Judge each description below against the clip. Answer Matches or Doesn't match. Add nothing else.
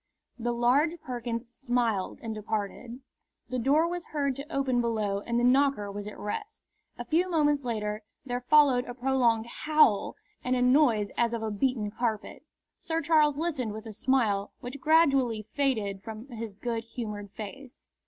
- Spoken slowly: Doesn't match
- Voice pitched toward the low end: Doesn't match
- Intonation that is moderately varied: Matches